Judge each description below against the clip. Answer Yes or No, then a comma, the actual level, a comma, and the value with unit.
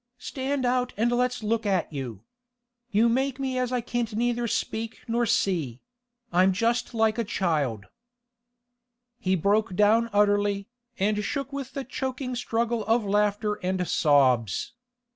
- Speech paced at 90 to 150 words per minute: Yes, average, 140 wpm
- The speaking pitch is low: No, high, 225 Hz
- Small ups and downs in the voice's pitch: No, average, 3.9 semitones